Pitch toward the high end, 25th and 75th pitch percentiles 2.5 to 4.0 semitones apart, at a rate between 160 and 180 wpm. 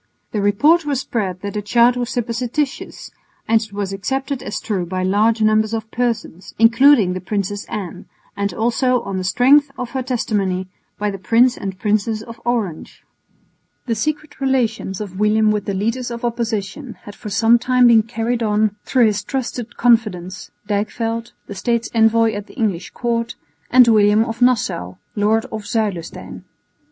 Yes: high, 220 Hz; average, 2.8 semitones; average, 165 wpm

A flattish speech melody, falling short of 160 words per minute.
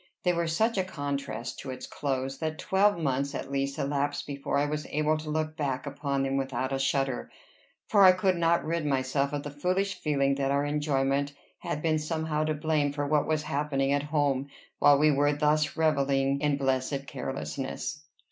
No: narrow, 2.0 semitones; average, 190 wpm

